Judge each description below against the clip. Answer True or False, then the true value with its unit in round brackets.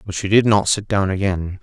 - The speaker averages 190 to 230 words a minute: False (260 wpm)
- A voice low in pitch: True (100 Hz)